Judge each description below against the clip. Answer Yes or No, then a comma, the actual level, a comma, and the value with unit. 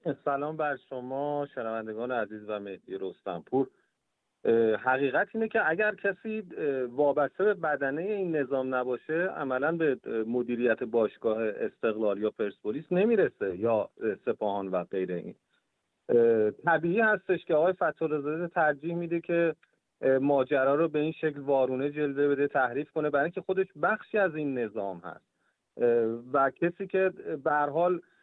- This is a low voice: No, medium, 145 Hz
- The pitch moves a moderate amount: No, wide, 5.7 semitones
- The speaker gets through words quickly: No, average, 135 wpm